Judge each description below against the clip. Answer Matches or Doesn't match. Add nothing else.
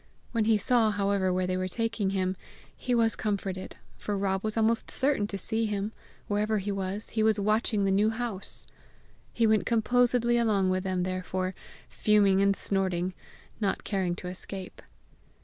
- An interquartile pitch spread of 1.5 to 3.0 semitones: Matches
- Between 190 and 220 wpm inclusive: Doesn't match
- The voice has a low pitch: Doesn't match